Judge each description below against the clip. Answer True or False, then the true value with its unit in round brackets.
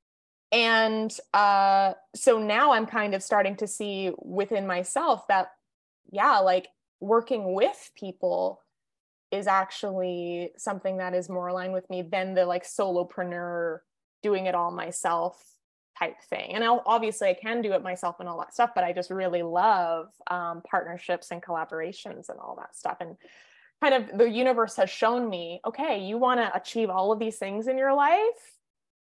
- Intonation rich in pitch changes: False (4.0 semitones)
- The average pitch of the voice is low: False (195 Hz)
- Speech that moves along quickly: False (170 wpm)